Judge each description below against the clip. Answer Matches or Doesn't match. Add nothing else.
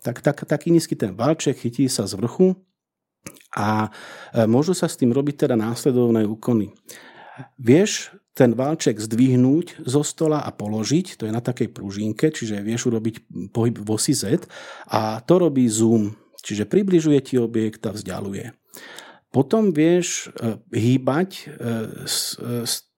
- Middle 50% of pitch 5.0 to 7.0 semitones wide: Matches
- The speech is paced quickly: Doesn't match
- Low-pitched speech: Matches